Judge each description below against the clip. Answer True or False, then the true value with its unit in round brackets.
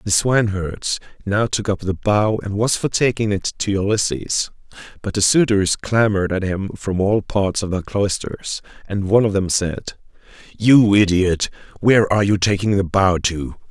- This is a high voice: False (100 Hz)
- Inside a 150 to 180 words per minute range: True (175 wpm)